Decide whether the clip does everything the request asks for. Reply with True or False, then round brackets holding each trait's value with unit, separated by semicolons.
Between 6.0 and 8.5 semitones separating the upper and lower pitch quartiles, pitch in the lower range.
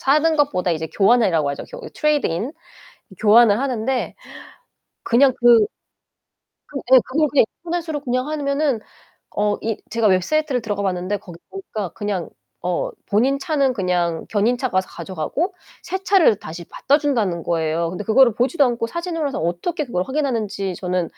False (7.3 semitones; 230 Hz)